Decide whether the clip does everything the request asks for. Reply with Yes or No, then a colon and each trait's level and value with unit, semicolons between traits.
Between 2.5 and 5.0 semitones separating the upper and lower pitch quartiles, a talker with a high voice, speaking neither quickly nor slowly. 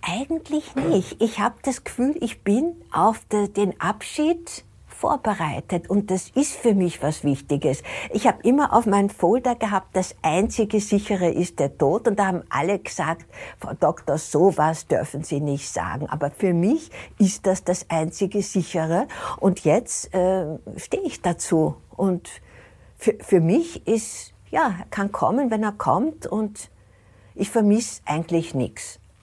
No: wide, 5.6 semitones; high, 195 Hz; average, 155 wpm